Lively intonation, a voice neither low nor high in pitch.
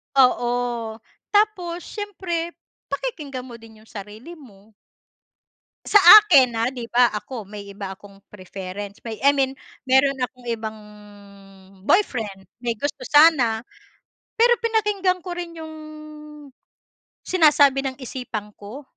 No: wide, 7.1 semitones; very high, 255 Hz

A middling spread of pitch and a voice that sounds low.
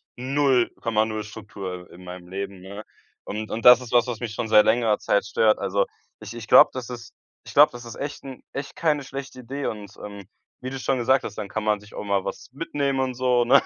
Yes: average, 3.8 semitones; low, 115 Hz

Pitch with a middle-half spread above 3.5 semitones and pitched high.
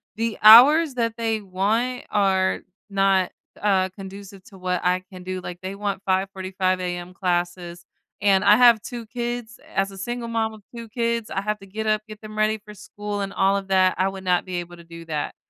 No: average, 2.8 semitones; high, 195 Hz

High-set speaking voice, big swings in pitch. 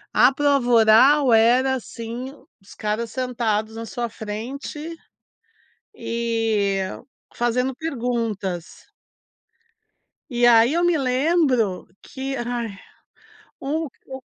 No: high, 240 Hz; average, 3.0 semitones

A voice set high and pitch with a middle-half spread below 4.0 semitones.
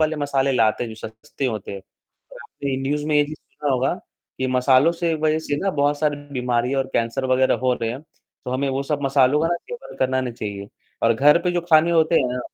No: low, 135 Hz; average, 3.1 semitones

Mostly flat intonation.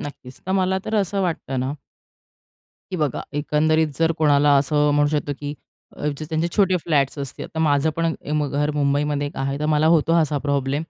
Yes: narrow, 2.2 semitones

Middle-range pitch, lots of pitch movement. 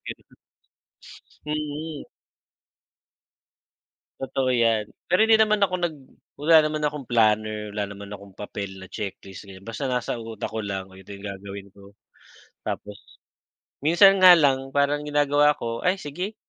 No: low, 125 Hz; wide, 6.9 semitones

